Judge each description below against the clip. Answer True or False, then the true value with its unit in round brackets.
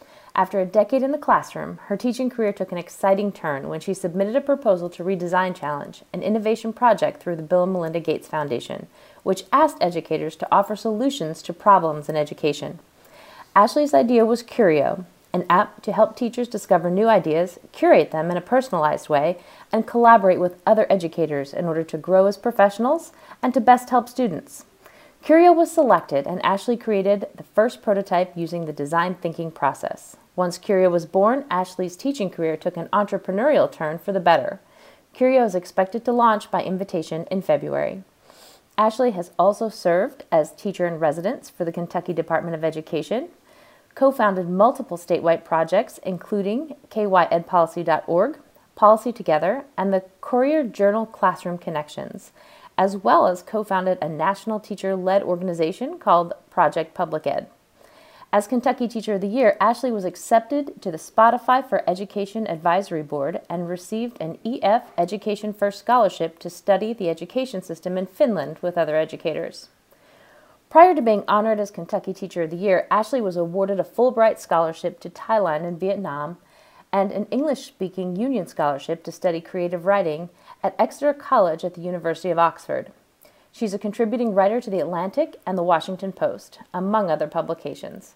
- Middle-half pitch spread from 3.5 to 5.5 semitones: True (4.6 semitones)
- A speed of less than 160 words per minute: False (165 wpm)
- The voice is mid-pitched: False (195 Hz)